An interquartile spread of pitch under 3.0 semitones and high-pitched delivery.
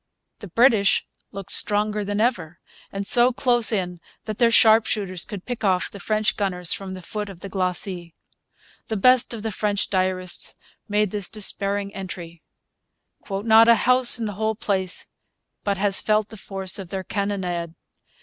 Yes: narrow, 2.6 semitones; high, 200 Hz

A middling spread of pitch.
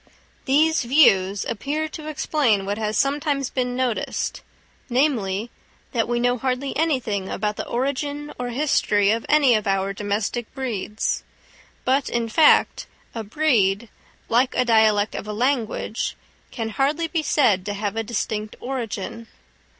Yes: average, 4.6 semitones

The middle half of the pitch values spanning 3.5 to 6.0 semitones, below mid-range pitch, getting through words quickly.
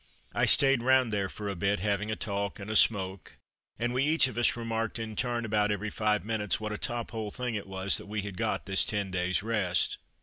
No: narrow, 2.5 semitones; low, 105 Hz; fast, 235 wpm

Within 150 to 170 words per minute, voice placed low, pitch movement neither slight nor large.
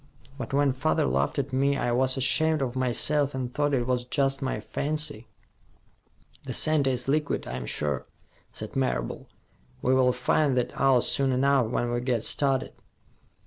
No: average, 165 wpm; low, 130 Hz; narrow, 2.3 semitones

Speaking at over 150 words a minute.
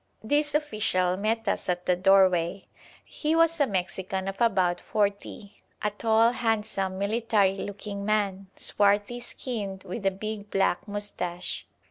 No: slow, 135 wpm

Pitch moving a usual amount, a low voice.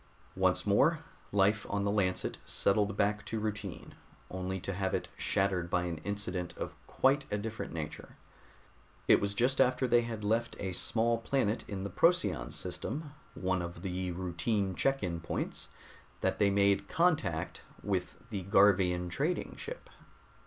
Yes: average, 3.6 semitones; low, 100 Hz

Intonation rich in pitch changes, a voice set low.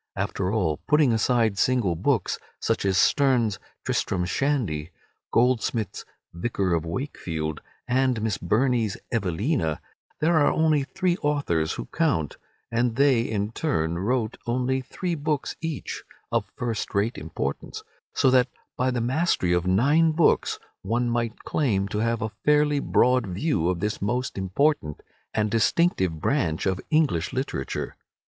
Yes: wide, 6.7 semitones; low, 115 Hz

